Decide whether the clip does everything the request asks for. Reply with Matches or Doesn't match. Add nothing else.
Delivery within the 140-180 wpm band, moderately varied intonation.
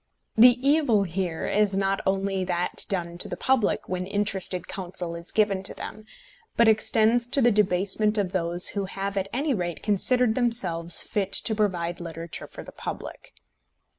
Matches